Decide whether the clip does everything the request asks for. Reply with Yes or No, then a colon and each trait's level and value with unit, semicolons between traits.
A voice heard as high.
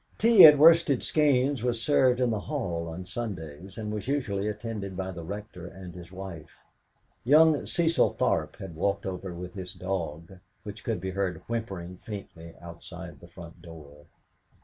No: very low, 95 Hz